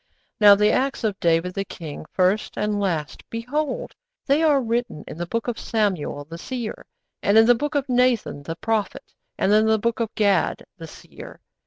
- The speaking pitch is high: Yes, high, 215 Hz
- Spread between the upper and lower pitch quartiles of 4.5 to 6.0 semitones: Yes, average, 4.8 semitones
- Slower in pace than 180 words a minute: No, average, 190 wpm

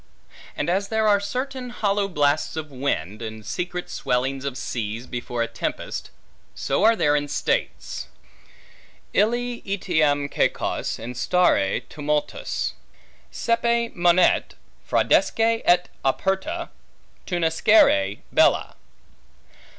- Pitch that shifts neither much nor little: No, wide, 8.0 semitones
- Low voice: No, medium, 170 Hz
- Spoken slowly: Yes, slow, 105 wpm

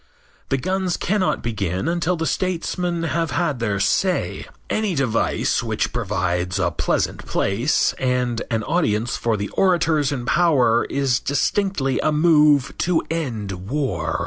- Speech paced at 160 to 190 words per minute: No, average, 140 wpm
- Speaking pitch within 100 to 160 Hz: Yes, medium, 140 Hz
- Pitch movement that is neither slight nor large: No, wide, 7.1 semitones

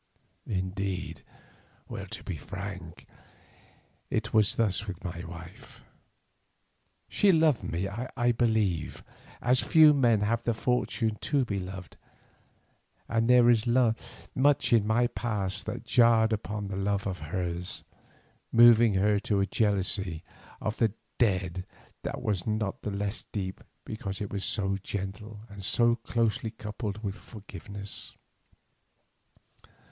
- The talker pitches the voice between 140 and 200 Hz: No, low, 105 Hz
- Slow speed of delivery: Yes, slow, 125 wpm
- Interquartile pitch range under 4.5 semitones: Yes, average, 3.2 semitones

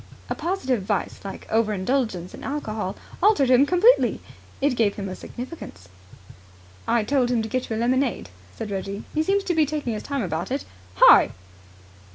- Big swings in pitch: Yes, wide, 5.7 semitones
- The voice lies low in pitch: No, high, 245 Hz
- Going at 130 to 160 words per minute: No, average, 180 wpm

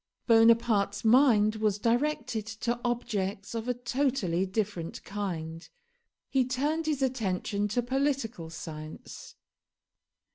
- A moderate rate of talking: No, slow, 105 wpm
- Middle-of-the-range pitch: No, high, 225 Hz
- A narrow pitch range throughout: No, average, 4.0 semitones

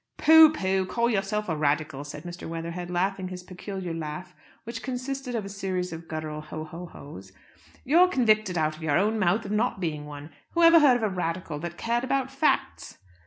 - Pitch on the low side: No, medium, 185 Hz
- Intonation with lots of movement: Yes, wide, 6.1 semitones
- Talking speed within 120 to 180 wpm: No, average, 195 wpm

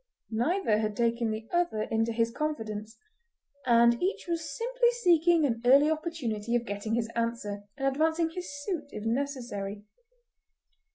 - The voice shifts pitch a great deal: Yes, wide, 6.3 semitones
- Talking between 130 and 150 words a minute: Yes, average, 145 wpm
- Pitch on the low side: No, high, 240 Hz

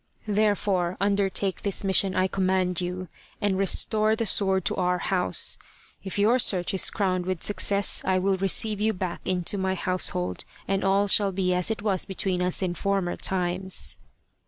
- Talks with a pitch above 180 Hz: Yes, high, 190 Hz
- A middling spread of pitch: No, narrow, 1.7 semitones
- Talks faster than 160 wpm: Yes, average, 170 wpm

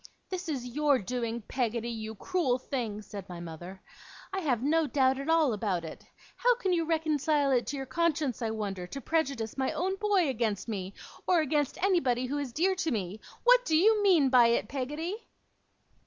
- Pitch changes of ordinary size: No, wide, 6.3 semitones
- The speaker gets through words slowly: No, average, 190 wpm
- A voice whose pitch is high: Yes, very high, 270 Hz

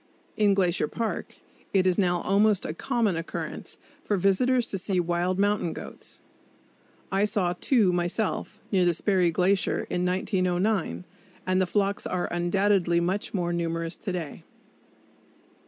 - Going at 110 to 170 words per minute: Yes, average, 140 wpm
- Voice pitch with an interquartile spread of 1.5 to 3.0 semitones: Yes, narrow, 2.5 semitones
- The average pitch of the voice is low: No, medium, 185 Hz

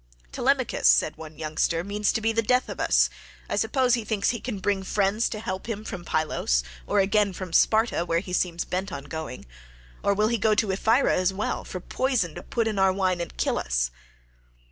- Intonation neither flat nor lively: Yes, average, 4.1 semitones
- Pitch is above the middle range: Yes, high, 195 Hz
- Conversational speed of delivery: No, fast, 210 wpm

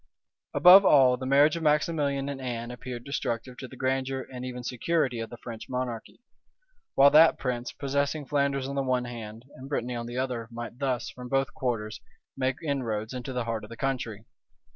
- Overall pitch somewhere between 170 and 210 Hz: No, low, 130 Hz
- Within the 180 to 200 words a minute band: Yes, average, 190 wpm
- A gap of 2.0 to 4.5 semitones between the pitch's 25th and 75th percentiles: Yes, narrow, 2.5 semitones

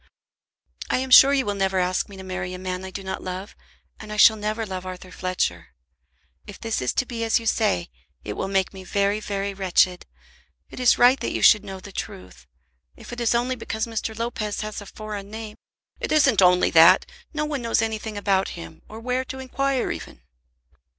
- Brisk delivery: Yes, fast, 210 wpm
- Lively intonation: No, average, 3.6 semitones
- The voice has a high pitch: Yes, high, 205 Hz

